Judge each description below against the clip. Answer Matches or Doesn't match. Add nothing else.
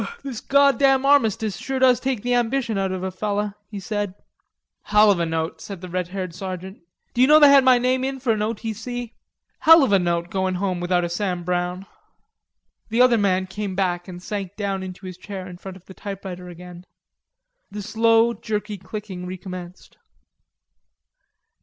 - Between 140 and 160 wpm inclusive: Doesn't match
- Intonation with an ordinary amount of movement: Matches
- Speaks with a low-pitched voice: Doesn't match